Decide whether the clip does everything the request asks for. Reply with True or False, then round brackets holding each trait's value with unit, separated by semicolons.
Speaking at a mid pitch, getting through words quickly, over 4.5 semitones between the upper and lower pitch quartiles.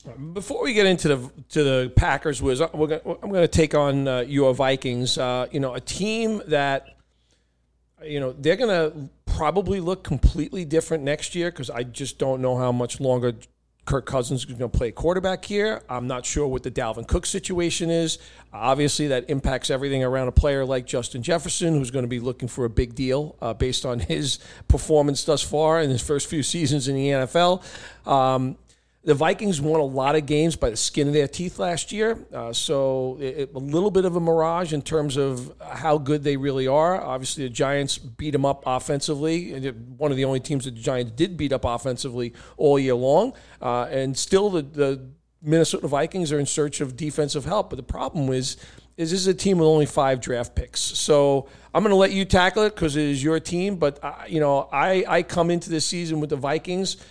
False (145 Hz; 215 wpm; 3.8 semitones)